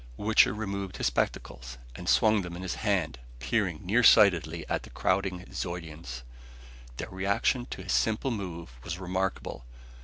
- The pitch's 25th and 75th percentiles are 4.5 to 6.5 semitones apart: No, average, 3.5 semitones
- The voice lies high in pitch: No, very low, 95 Hz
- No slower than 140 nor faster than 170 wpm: Yes, average, 150 wpm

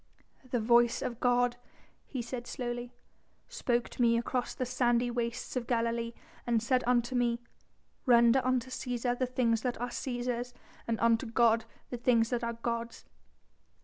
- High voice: Yes, high, 240 Hz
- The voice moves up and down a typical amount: No, narrow, 1.1 semitones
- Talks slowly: No, average, 155 wpm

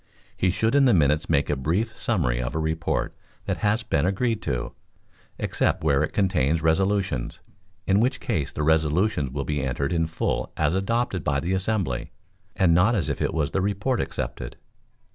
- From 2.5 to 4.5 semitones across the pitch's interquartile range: No, wide, 5.6 semitones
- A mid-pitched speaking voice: No, very low, 85 Hz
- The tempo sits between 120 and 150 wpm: No, average, 180 wpm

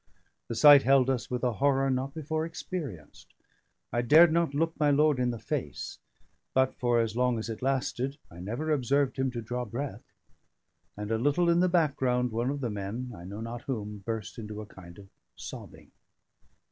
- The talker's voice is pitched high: No, low, 125 Hz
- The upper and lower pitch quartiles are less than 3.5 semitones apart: No, average, 4.1 semitones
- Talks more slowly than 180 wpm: No, average, 190 wpm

